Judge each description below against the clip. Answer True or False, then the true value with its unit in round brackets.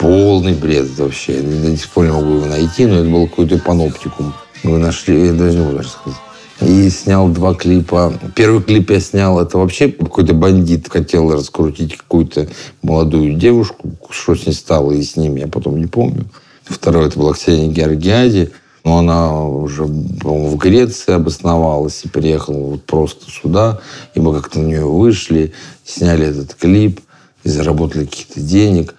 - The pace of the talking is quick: True (165 wpm)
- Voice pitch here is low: True (85 Hz)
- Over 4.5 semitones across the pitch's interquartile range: False (2.9 semitones)